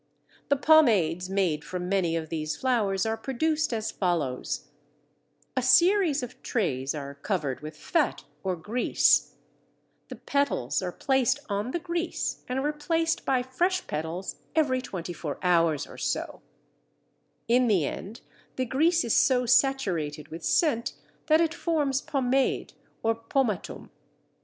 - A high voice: Yes, high, 235 Hz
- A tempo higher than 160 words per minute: No, average, 140 wpm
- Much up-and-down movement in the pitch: Yes, wide, 8.3 semitones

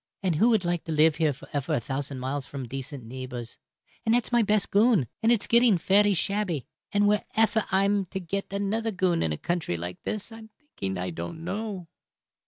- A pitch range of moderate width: No, wide, 7.4 semitones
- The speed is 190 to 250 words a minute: Yes, average, 200 wpm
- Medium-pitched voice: Yes, medium, 180 Hz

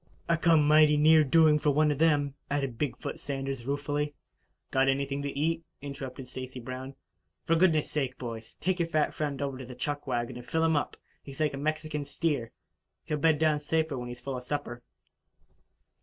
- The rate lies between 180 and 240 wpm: Yes, average, 195 wpm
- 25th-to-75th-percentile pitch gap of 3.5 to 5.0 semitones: No, average, 2.7 semitones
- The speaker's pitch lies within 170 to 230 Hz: No, medium, 145 Hz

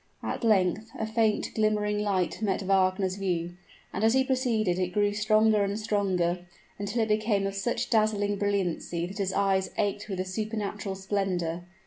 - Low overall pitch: No, high, 200 Hz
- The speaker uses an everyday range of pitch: No, narrow, 2.3 semitones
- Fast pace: No, average, 165 wpm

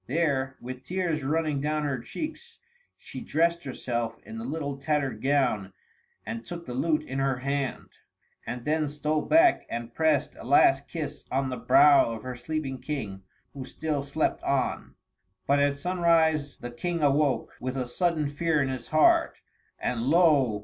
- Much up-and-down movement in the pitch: No, average, 3.5 semitones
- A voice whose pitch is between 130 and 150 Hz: Yes, medium, 140 Hz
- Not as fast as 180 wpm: Yes, average, 165 wpm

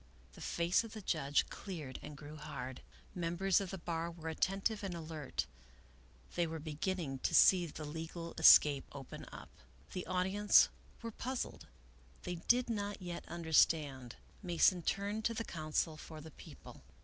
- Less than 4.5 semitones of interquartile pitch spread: Yes, average, 3.7 semitones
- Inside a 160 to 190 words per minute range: Yes, average, 165 wpm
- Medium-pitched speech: Yes, medium, 170 Hz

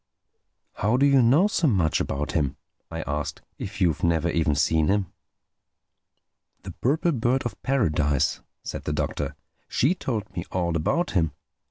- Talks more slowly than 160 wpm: Yes, average, 145 wpm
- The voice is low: Yes, very low, 95 Hz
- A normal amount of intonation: No, wide, 8.2 semitones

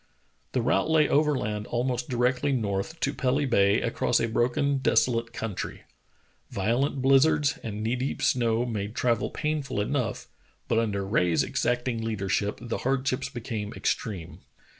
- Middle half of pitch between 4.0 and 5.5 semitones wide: No, average, 3.6 semitones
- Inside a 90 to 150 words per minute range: Yes, average, 140 wpm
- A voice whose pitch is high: No, low, 120 Hz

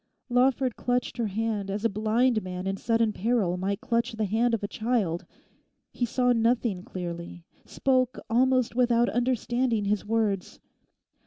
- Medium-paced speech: Yes, average, 150 wpm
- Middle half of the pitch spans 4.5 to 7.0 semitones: No, average, 3.5 semitones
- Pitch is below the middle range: No, high, 225 Hz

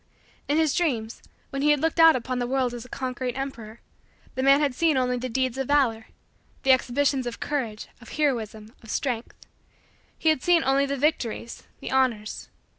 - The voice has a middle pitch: No, very high, 260 Hz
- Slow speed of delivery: No, average, 190 wpm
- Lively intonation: No, average, 3.0 semitones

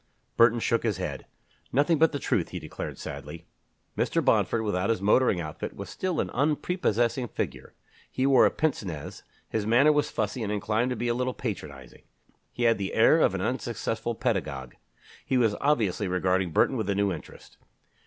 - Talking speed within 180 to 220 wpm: Yes, average, 185 wpm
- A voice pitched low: Yes, low, 115 Hz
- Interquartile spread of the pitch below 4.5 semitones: No, average, 5.2 semitones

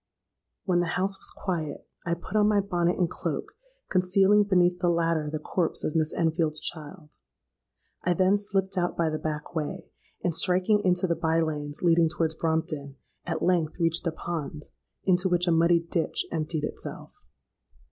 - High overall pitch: No, medium, 170 Hz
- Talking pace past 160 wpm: Yes, average, 170 wpm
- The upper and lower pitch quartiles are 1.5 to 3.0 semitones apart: Yes, narrow, 2.4 semitones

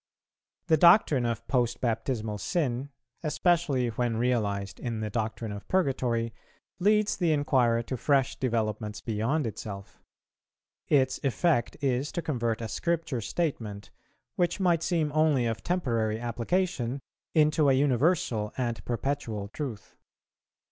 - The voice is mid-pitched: No, low, 125 Hz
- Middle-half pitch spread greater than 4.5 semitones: Yes, average, 5.2 semitones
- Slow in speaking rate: Yes, slow, 125 wpm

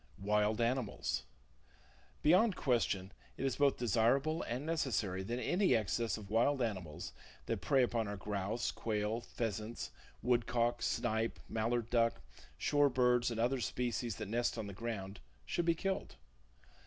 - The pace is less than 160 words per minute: Yes, average, 150 wpm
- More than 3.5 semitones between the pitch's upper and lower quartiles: No, average, 3.1 semitones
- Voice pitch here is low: Yes, low, 115 Hz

